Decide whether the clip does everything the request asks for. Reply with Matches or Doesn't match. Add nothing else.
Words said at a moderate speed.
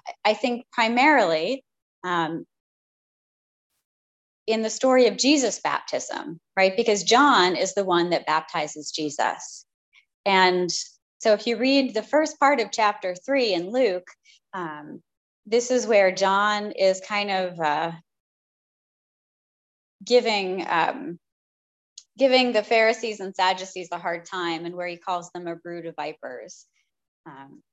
Doesn't match